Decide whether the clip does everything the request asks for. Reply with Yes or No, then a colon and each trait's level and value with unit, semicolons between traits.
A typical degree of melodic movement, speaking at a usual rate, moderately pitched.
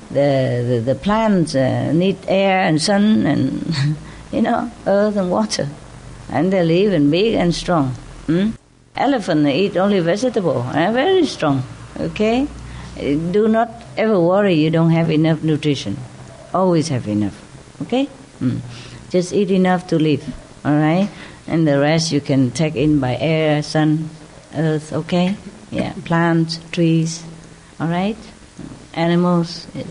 Yes: average, 4.5 semitones; average, 145 wpm; medium, 165 Hz